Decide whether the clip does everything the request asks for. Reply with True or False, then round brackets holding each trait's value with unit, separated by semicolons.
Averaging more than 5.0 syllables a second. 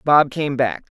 False (3.8 syllables/s)